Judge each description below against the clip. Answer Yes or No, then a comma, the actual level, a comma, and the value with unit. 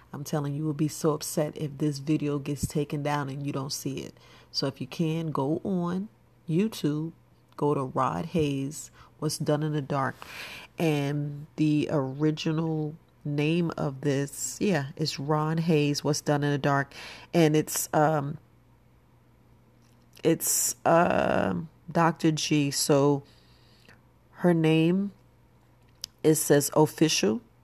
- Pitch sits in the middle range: Yes, medium, 150 Hz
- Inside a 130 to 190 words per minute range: Yes, average, 140 wpm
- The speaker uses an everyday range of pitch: No, narrow, 2.2 semitones